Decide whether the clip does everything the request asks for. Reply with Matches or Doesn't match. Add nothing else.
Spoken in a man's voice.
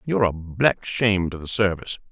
Matches